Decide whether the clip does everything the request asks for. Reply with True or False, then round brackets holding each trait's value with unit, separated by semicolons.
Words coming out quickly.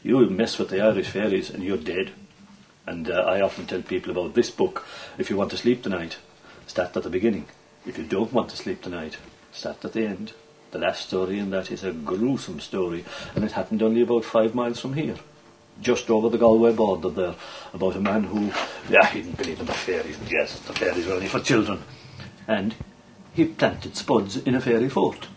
True (210 wpm)